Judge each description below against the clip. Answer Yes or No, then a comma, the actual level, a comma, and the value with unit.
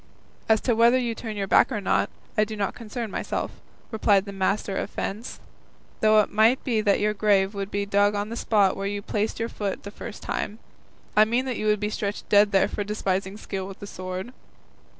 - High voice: Yes, high, 210 Hz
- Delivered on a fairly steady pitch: Yes, narrow, 1.8 semitones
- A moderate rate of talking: No, fast, 220 wpm